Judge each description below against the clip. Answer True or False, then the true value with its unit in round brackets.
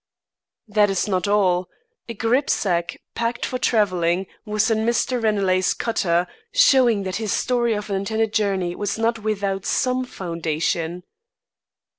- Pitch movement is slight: False (3.6 semitones)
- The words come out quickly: False (140 wpm)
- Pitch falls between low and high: False (205 Hz)